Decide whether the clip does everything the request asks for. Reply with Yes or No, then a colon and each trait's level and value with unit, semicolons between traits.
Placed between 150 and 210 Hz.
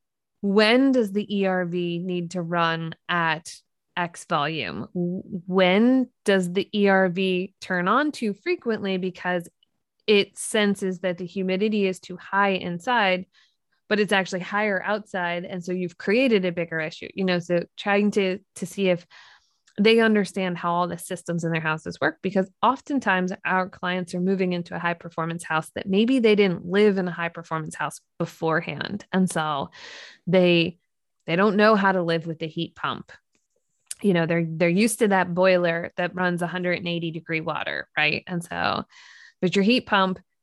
Yes: medium, 185 Hz